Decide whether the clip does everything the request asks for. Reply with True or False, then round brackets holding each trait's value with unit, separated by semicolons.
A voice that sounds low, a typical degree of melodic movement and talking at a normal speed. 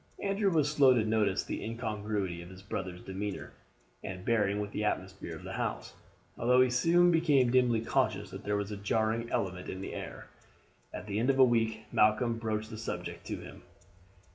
True (110 Hz; 3.5 semitones; 190 wpm)